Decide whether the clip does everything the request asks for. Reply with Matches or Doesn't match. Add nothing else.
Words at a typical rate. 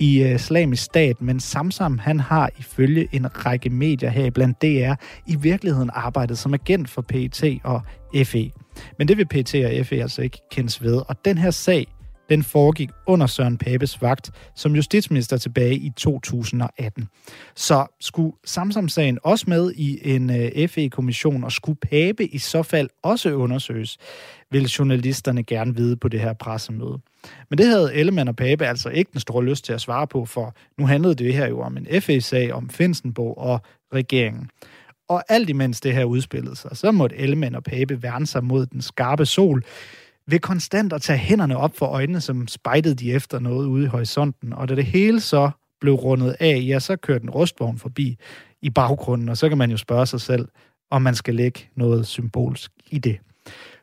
Matches